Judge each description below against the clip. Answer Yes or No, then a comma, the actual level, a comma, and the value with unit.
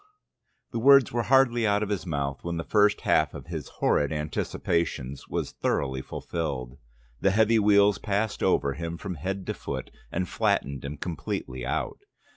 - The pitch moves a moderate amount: No, wide, 6.5 semitones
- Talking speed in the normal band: Yes, average, 165 wpm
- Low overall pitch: Yes, very low, 90 Hz